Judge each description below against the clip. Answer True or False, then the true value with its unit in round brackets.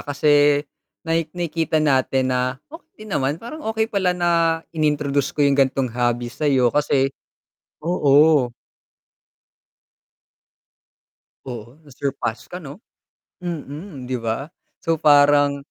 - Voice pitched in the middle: True (145 Hz)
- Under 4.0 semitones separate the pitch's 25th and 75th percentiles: True (3.5 semitones)